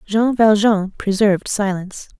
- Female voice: Yes, female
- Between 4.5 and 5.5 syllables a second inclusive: Yes, 4.6 syllables/s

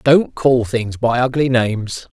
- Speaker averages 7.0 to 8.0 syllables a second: No, 4.0 syllables/s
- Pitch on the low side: Yes, low, 120 Hz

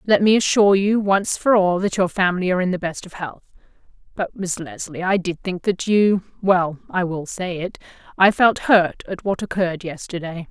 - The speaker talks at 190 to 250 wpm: Yes, average, 200 wpm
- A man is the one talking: No, female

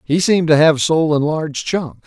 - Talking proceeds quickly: Yes, fast, 235 wpm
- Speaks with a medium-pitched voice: Yes, medium, 155 Hz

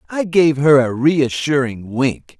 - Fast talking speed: No, average, 150 wpm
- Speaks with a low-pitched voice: No, medium, 155 Hz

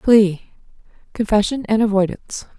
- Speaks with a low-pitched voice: No, high, 210 Hz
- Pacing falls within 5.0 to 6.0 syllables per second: No, 4.7 syllables/s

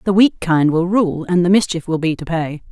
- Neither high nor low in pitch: Yes, medium, 175 Hz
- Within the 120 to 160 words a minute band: No, fast, 265 wpm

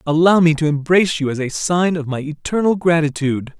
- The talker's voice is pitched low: No, medium, 160 Hz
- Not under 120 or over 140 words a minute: No, average, 200 wpm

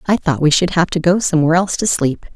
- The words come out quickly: Yes, fast, 280 wpm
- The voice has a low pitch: No, medium, 170 Hz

